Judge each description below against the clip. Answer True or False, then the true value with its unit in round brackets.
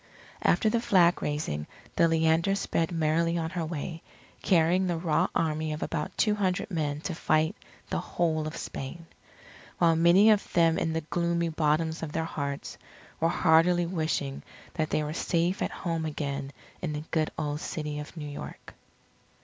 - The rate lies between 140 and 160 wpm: False (170 wpm)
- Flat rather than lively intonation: True (1.9 semitones)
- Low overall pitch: False (160 Hz)